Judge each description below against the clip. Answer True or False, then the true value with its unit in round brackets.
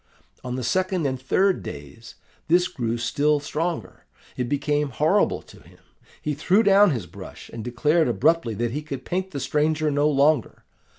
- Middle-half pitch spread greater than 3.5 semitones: True (5.0 semitones)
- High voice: False (145 Hz)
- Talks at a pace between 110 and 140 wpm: False (170 wpm)